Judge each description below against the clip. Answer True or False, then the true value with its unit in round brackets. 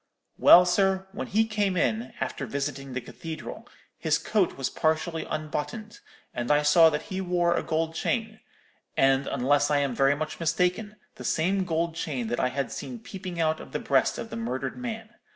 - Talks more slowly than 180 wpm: False (190 wpm)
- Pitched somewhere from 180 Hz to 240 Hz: False (160 Hz)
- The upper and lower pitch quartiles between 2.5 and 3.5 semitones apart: False (5.2 semitones)